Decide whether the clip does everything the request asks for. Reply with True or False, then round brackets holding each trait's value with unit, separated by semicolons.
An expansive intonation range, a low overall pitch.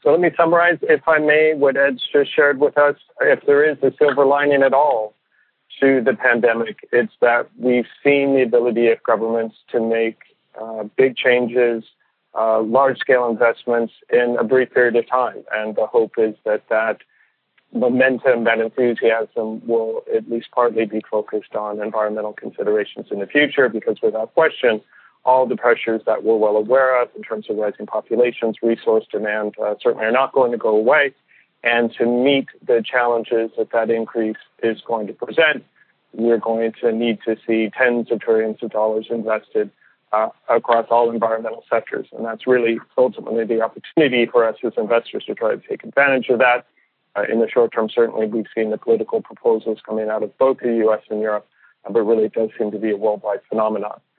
False (3.8 semitones; 120 Hz)